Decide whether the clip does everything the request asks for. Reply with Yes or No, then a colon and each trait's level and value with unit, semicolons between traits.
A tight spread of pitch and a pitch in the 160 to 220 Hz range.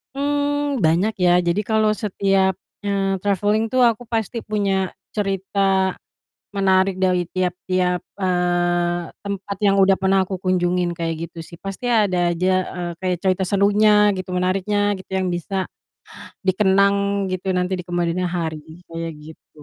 Yes: narrow, 2.1 semitones; high, 190 Hz